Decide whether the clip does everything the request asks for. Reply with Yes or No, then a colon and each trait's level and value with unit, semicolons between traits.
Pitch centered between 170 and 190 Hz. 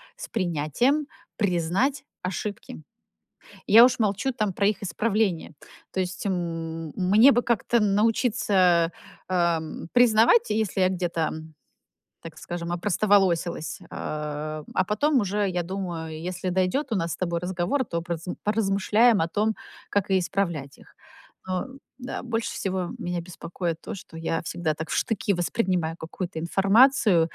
Yes: medium, 185 Hz